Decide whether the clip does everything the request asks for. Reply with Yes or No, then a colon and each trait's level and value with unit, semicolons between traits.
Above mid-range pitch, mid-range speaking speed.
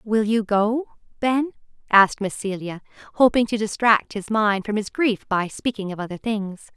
Yes: high, 215 Hz; average, 180 wpm